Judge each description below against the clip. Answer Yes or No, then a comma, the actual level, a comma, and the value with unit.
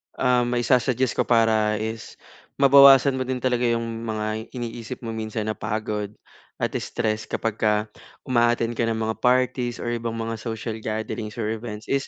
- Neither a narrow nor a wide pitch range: No, narrow, 2.0 semitones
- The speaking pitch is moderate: No, low, 115 Hz